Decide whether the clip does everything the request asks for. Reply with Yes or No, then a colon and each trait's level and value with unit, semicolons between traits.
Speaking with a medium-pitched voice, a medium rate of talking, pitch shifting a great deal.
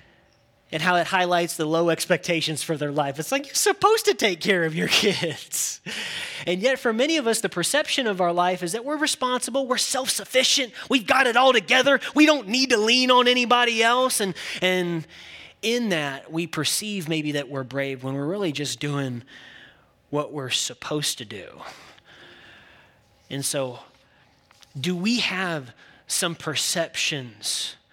Yes: medium, 180 Hz; average, 170 wpm; wide, 8.6 semitones